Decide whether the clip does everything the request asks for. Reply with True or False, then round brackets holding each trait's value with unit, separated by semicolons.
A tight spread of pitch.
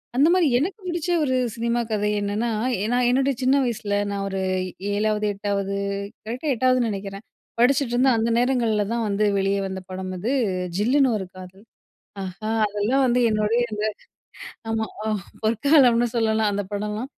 False (3.7 semitones)